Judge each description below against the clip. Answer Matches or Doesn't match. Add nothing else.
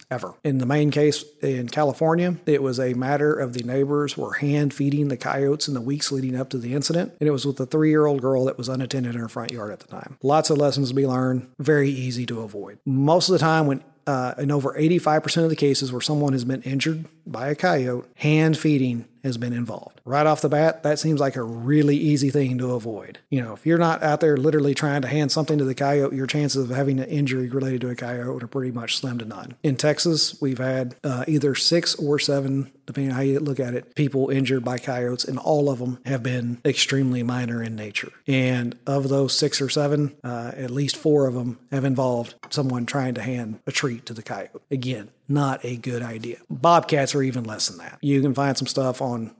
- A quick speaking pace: Matches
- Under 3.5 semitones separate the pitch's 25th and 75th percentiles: Matches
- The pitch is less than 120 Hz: Doesn't match